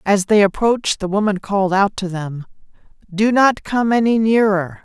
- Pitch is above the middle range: Yes, high, 205 Hz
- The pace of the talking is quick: No, average, 175 wpm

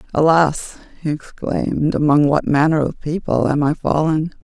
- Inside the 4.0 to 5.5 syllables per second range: Yes, 4.7 syllables/s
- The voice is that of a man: No, female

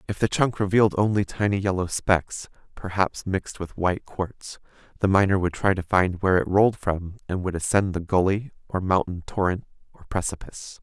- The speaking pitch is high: No, very low, 95 Hz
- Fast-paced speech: No, average, 185 wpm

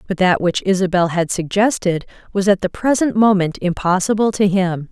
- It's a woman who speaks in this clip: Yes, female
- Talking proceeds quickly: No, average, 170 wpm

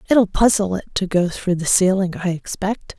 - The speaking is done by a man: No, female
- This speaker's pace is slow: No, average, 200 wpm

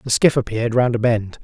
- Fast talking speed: Yes, fast, 250 wpm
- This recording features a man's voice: Yes, male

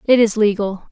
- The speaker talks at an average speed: Yes, average, 195 wpm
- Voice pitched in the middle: No, high, 215 Hz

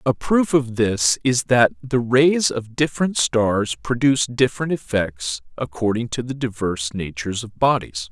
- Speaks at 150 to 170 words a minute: Yes, average, 155 wpm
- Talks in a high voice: No, low, 120 Hz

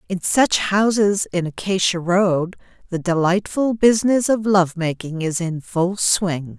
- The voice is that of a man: No, female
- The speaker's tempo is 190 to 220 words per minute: No, average, 145 wpm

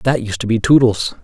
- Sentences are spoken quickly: Yes, fast, 245 wpm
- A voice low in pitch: Yes, low, 115 Hz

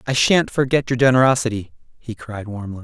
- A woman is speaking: No, male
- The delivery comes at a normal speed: Yes, average, 170 wpm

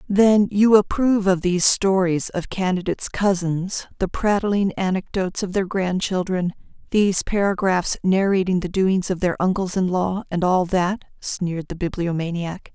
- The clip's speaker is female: Yes, female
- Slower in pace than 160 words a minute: Yes, average, 145 wpm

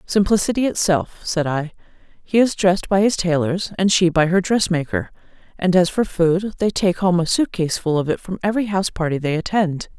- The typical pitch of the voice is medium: Yes, medium, 180 Hz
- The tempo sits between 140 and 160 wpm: No, fast, 205 wpm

